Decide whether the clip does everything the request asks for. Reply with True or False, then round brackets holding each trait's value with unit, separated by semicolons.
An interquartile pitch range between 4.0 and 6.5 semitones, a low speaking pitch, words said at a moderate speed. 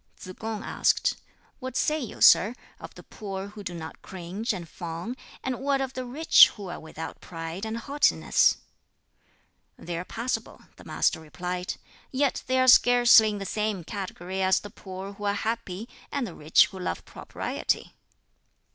False (5.2 semitones; 205 Hz; 170 wpm)